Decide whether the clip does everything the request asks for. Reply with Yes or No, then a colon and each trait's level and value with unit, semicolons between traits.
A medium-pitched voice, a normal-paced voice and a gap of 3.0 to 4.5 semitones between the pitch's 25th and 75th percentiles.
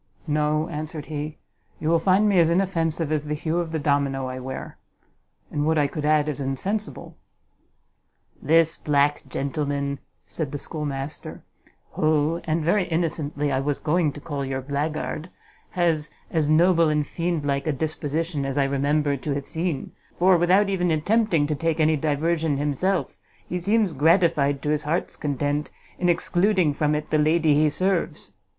No: medium, 155 Hz; average, 170 wpm; narrow, 2.6 semitones